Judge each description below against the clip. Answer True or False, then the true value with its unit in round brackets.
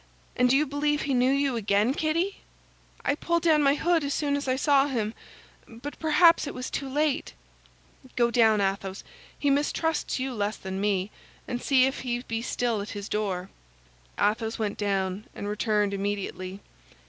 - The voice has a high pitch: True (245 Hz)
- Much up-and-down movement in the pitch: True (5.7 semitones)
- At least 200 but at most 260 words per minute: False (170 wpm)